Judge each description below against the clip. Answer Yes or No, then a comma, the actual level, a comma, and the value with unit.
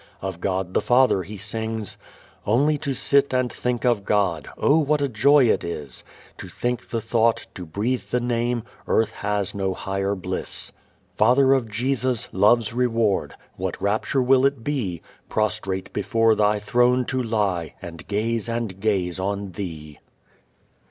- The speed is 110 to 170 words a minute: Yes, average, 155 wpm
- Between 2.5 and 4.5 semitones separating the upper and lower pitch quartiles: Yes, average, 4.0 semitones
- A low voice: Yes, low, 110 Hz